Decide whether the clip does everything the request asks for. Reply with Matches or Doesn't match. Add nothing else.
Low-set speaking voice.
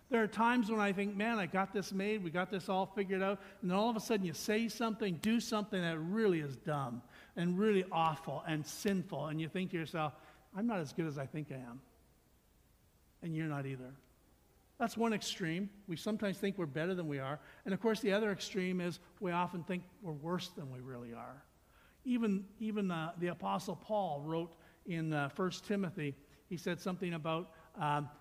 Doesn't match